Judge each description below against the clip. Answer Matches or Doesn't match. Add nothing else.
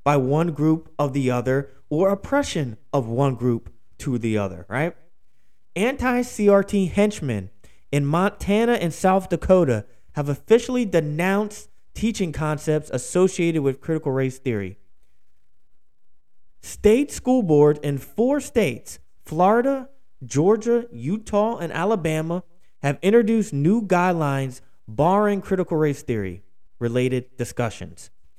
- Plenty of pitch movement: Matches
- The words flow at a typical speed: Doesn't match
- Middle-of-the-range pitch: Matches